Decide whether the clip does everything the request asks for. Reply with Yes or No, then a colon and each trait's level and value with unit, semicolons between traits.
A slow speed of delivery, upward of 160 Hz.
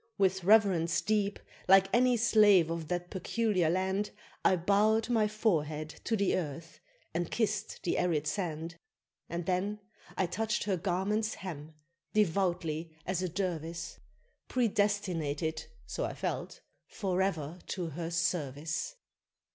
Yes: slow, 125 wpm; medium, 185 Hz